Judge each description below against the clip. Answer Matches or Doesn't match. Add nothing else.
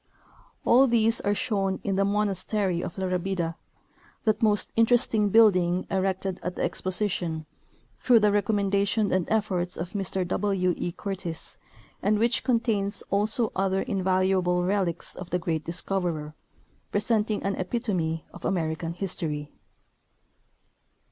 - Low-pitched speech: Doesn't match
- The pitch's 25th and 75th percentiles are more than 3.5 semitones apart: Doesn't match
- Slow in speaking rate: Matches